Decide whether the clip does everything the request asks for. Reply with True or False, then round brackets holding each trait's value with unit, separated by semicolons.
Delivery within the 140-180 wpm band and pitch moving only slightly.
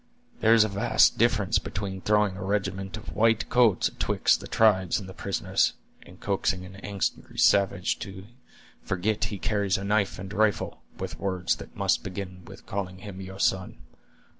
True (170 wpm; 1.7 semitones)